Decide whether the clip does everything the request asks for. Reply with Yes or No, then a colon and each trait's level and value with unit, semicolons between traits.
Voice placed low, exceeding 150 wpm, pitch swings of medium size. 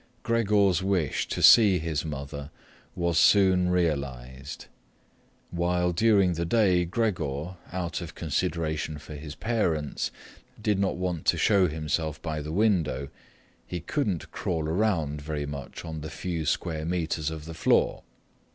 No: very low, 85 Hz; average, 140 wpm; average, 3.3 semitones